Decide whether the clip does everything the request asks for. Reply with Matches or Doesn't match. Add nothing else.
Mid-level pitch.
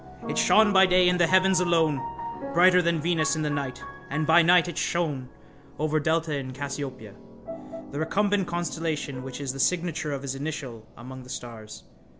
Matches